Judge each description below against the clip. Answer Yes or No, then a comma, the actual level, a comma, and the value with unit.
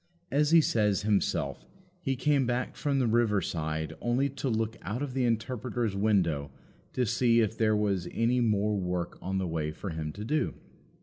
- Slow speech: No, average, 185 wpm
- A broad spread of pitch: No, average, 4.7 semitones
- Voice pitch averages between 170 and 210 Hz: No, low, 110 Hz